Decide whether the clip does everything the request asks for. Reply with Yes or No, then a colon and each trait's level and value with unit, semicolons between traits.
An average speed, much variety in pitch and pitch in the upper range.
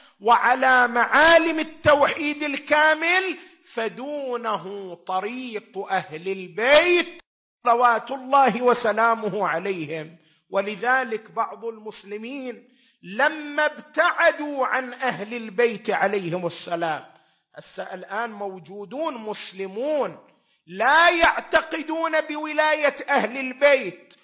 Yes: average, 75 wpm; wide, 6.4 semitones; high, 245 Hz